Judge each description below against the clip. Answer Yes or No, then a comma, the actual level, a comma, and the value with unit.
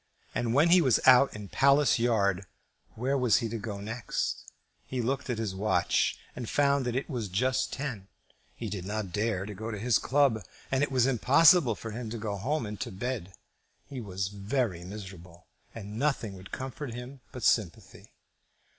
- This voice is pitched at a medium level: No, low, 115 Hz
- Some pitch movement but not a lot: Yes, average, 4.4 semitones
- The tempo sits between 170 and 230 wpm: Yes, average, 185 wpm